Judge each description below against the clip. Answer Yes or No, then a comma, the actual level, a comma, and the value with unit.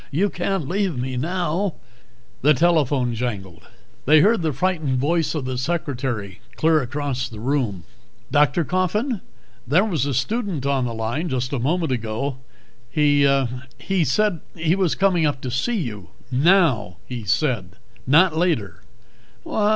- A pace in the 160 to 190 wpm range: No, average, 150 wpm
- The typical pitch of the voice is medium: Yes, medium, 145 Hz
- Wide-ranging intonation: Yes, wide, 5.9 semitones